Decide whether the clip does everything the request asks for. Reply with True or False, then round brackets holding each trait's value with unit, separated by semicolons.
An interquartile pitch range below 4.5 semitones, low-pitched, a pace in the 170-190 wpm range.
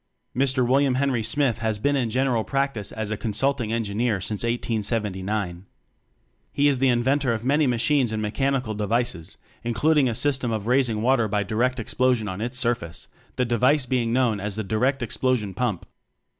True (3.3 semitones; 120 Hz; 175 wpm)